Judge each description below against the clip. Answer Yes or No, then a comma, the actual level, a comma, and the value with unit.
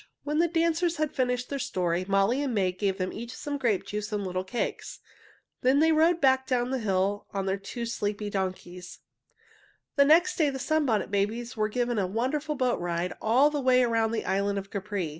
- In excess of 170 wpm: Yes, average, 200 wpm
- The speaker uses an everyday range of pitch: No, wide, 5.8 semitones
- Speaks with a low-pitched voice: No, high, 230 Hz